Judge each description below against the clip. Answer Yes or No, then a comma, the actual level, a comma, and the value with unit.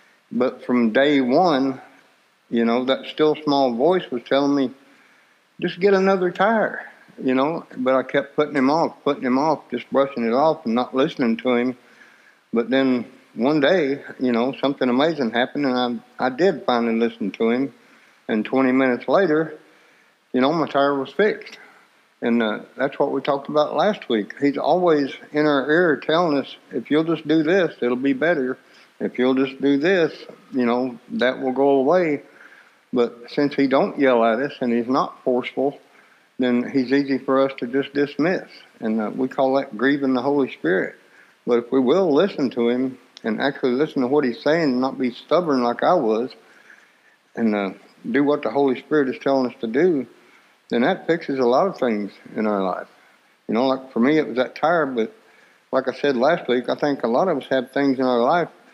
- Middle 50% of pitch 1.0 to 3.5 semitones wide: Yes, narrow, 2.5 semitones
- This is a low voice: Yes, low, 130 Hz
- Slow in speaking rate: No, average, 200 wpm